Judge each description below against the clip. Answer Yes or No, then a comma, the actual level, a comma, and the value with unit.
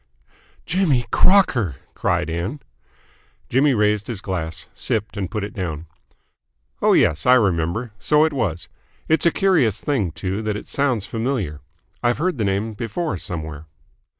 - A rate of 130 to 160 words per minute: Yes, average, 150 wpm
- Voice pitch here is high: No, low, 105 Hz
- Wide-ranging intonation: Yes, wide, 6.8 semitones